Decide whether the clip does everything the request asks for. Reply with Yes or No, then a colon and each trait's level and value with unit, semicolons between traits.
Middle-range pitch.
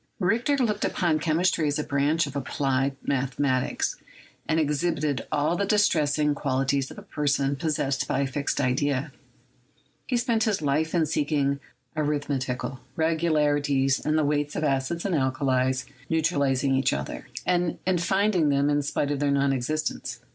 Yes: medium, 145 Hz